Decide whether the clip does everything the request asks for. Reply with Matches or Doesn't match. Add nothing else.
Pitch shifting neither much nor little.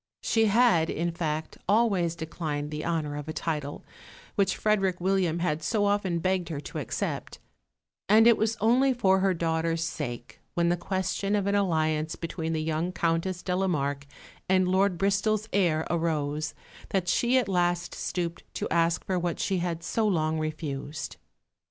Matches